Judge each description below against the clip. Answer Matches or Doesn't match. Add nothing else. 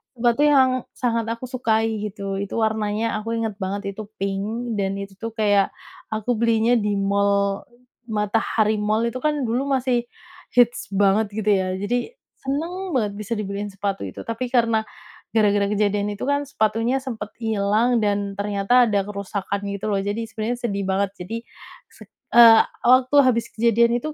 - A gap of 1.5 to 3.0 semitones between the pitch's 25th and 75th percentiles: Matches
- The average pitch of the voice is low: Doesn't match